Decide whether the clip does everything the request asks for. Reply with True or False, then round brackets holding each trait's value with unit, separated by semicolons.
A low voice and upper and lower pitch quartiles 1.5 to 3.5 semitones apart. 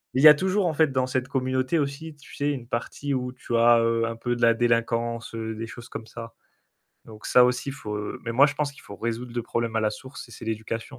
True (120 Hz; 3.1 semitones)